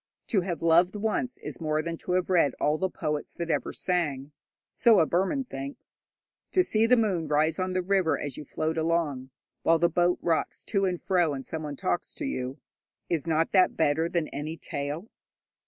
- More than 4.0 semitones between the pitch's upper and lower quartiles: No, average, 3.3 semitones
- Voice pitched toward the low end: No, medium, 170 Hz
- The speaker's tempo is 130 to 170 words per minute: No, average, 195 wpm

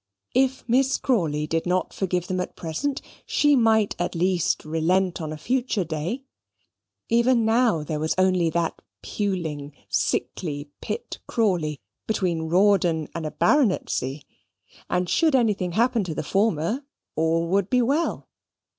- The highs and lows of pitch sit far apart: Yes, wide, 6.2 semitones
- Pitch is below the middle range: No, medium, 185 Hz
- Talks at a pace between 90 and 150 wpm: Yes, average, 140 wpm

